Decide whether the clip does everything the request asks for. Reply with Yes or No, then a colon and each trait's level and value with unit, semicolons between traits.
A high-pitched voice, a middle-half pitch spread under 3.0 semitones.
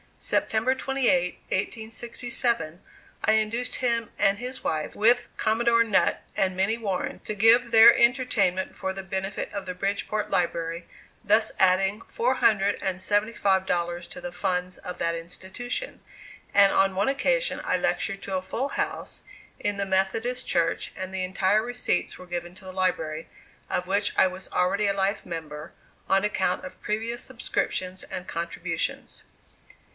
No: high, 195 Hz; average, 3.7 semitones